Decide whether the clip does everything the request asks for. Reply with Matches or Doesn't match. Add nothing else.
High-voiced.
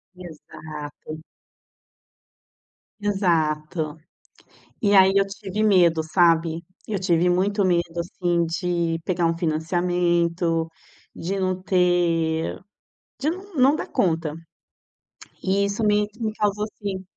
Doesn't match